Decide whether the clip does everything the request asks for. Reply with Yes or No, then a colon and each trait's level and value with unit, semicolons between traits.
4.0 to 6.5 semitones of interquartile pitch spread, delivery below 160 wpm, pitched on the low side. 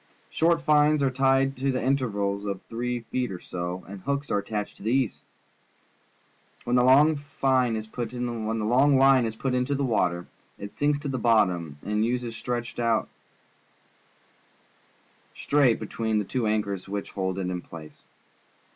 Yes: average, 4.6 semitones; average, 150 wpm; low, 120 Hz